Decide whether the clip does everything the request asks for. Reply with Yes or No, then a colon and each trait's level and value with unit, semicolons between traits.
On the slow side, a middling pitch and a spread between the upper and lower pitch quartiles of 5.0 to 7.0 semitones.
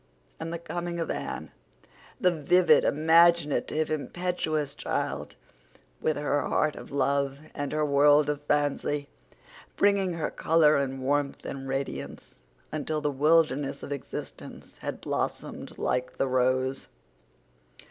No: slow, 125 wpm; medium, 150 Hz; narrow, 2.6 semitones